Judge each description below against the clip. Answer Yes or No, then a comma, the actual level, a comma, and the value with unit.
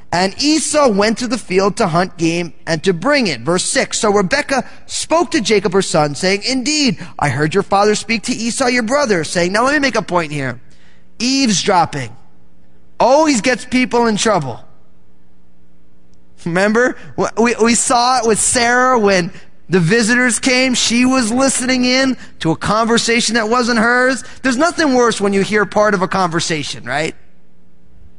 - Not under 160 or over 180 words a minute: Yes, average, 170 wpm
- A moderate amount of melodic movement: No, wide, 6.8 semitones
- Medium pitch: No, high, 210 Hz